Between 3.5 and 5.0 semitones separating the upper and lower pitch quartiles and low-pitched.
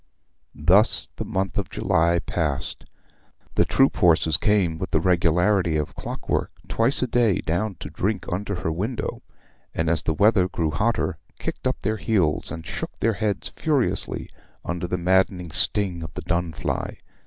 Yes: average, 3.8 semitones; very low, 90 Hz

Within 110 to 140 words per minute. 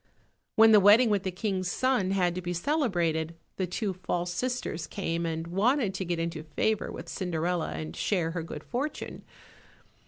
No: average, 175 wpm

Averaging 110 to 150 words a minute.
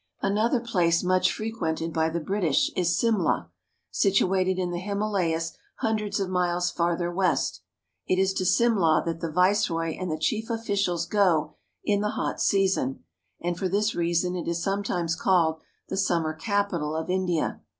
No: average, 160 wpm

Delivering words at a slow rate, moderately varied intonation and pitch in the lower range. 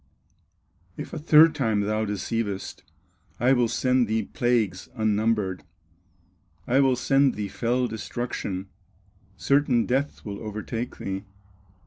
Yes: slow, 115 wpm; average, 3.6 semitones; low, 115 Hz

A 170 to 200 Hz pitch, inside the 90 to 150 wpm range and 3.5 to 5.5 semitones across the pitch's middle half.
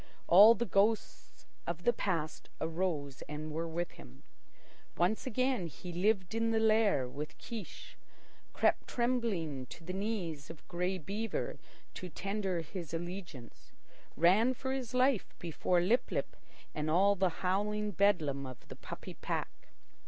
Yes: medium, 185 Hz; average, 145 wpm; average, 4.9 semitones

